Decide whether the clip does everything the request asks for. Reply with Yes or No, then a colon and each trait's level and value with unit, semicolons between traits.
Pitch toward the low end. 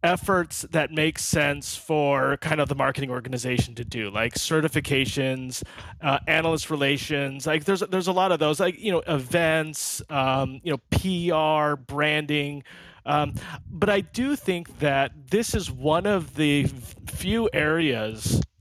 No: medium, 150 Hz